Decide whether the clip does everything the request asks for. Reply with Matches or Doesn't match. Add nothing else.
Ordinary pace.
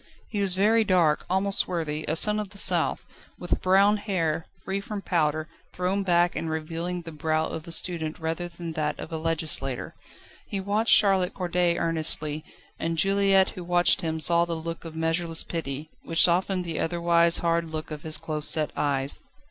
Matches